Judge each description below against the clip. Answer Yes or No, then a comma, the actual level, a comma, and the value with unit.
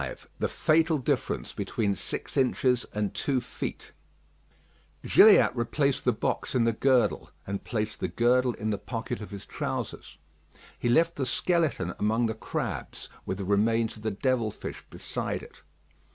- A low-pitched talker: Yes, low, 115 Hz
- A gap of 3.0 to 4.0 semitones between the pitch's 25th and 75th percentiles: Yes, average, 3.4 semitones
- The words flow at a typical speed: Yes, average, 160 wpm